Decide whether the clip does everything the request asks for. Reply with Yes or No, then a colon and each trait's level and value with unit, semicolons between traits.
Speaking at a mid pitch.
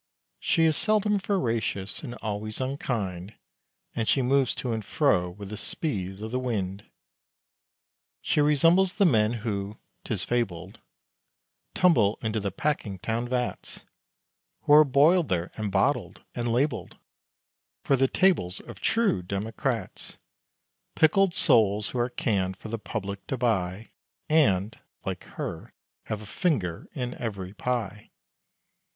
No: low, 115 Hz